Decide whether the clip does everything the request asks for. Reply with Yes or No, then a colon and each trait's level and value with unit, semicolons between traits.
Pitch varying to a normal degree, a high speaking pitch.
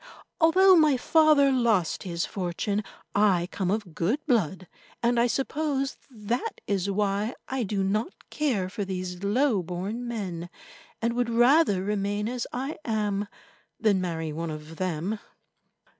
Yes: average, 4.9 semitones; high, 210 Hz